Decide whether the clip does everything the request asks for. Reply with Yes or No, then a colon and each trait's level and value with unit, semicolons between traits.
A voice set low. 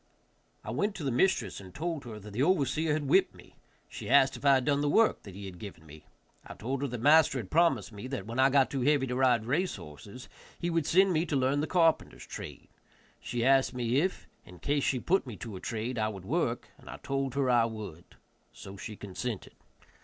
Yes: low, 130 Hz